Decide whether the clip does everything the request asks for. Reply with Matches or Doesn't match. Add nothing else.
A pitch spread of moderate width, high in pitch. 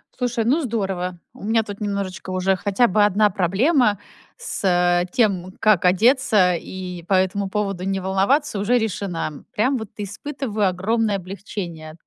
Matches